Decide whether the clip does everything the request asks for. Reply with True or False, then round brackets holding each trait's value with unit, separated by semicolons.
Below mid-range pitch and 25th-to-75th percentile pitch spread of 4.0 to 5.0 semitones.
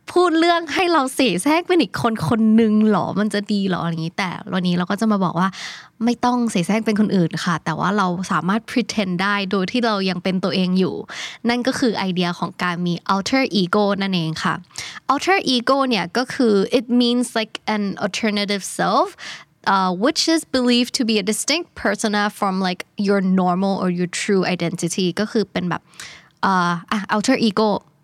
False (205 Hz; 4.5 semitones)